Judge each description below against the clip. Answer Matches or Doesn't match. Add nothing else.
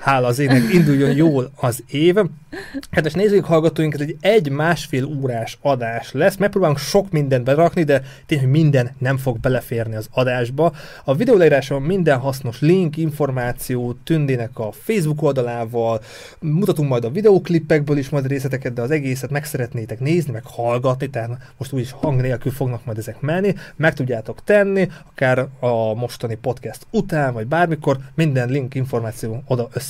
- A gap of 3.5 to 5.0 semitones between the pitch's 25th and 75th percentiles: Matches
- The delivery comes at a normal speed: Doesn't match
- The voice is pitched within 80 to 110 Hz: Doesn't match